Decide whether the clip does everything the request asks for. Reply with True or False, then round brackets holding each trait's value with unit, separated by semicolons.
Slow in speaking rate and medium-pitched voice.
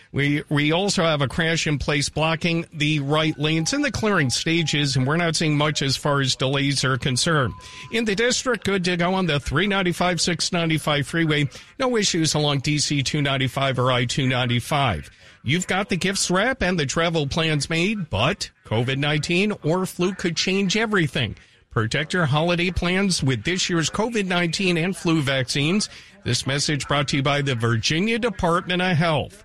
False (175 wpm; 160 Hz)